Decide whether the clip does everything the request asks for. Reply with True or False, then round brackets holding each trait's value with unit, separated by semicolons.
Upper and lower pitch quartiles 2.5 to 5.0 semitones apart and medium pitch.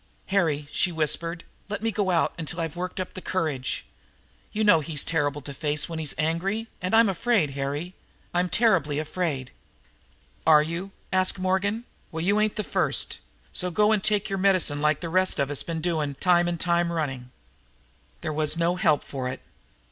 True (3.7 semitones; 170 Hz)